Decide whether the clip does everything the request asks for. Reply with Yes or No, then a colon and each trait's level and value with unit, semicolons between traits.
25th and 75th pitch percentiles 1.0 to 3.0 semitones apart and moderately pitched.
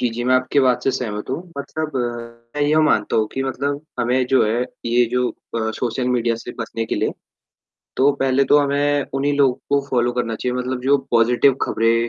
No: average, 2.7 semitones; low, 125 Hz